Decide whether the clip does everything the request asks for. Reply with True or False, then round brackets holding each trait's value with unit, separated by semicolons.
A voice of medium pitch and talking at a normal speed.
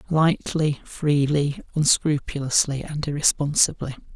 False (145 Hz; 70 wpm)